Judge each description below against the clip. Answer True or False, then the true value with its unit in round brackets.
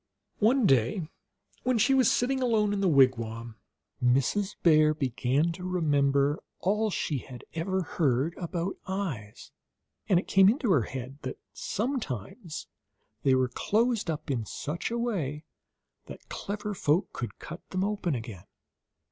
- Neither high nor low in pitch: True (165 Hz)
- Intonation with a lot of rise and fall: True (7.4 semitones)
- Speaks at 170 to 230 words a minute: False (145 wpm)